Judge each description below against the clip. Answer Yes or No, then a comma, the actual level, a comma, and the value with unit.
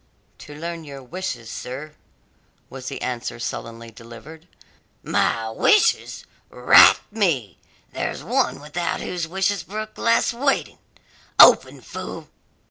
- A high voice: No, medium, 150 Hz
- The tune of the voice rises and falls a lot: Yes, wide, 7.7 semitones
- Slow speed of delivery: Yes, slow, 115 wpm